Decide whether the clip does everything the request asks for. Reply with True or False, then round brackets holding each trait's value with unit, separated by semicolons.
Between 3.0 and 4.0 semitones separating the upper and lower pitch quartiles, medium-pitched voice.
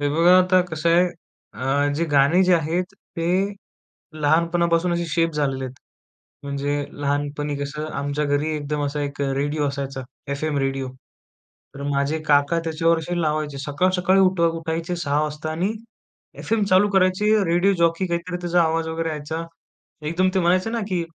True (3.3 semitones; 160 Hz)